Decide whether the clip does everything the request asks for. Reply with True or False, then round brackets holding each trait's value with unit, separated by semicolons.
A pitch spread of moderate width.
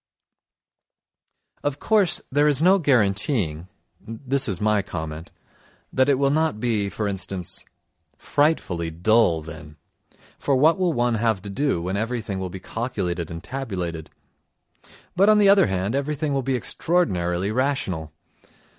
False (7.6 semitones)